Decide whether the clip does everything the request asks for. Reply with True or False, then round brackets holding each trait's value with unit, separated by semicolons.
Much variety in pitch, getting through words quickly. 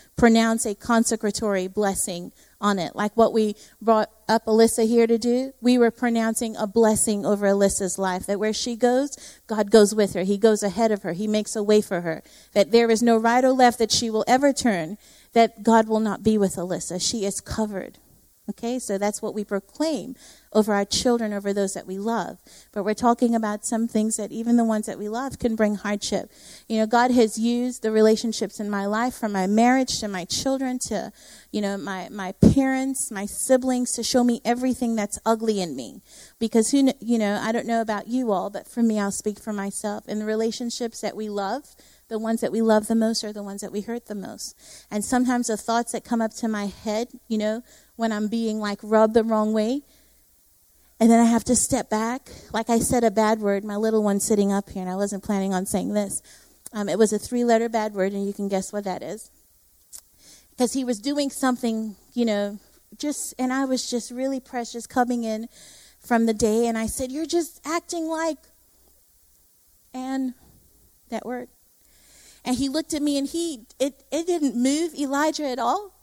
False (2.9 semitones; 210 wpm)